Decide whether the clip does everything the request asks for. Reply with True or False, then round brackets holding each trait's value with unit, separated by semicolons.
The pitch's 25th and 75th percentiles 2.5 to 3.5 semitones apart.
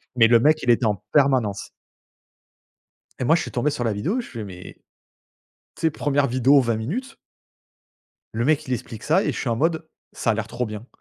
False (4.9 semitones)